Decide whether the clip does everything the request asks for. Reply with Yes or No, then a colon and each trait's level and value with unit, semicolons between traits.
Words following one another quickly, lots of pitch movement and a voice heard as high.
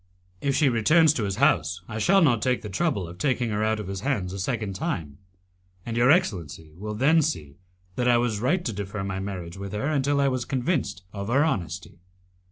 No: fast, 215 wpm; wide, 5.9 semitones; low, 110 Hz